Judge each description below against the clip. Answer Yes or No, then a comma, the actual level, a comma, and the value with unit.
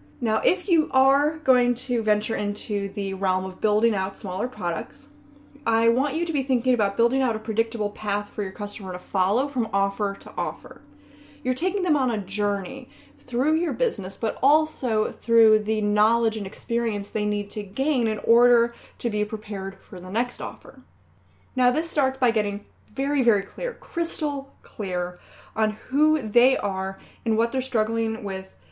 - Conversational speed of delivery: Yes, average, 175 wpm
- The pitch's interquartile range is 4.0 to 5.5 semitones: Yes, average, 4.3 semitones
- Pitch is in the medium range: No, high, 225 Hz